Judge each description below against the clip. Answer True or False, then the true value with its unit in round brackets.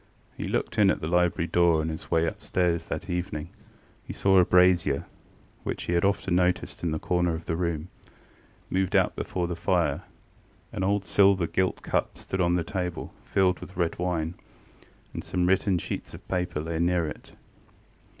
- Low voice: True (90 Hz)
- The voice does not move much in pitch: True (1.7 semitones)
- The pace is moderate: True (180 wpm)